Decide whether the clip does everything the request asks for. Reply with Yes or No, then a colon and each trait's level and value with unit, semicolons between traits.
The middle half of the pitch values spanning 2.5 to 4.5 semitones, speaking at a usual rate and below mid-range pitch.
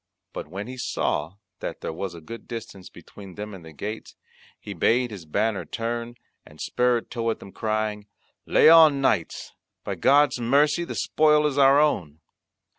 No: wide, 5.6 semitones; average, 170 wpm; low, 115 Hz